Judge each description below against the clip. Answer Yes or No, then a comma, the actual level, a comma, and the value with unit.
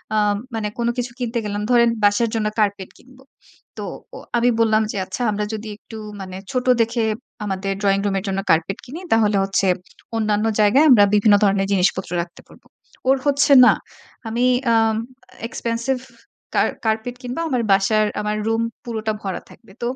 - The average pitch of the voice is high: Yes, high, 220 Hz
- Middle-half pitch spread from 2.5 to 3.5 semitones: Yes, average, 2.9 semitones